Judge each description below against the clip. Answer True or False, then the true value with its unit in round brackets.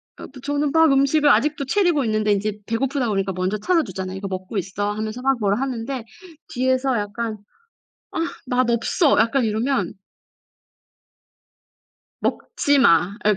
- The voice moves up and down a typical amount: True (4.9 semitones)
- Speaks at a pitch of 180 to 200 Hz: False (230 Hz)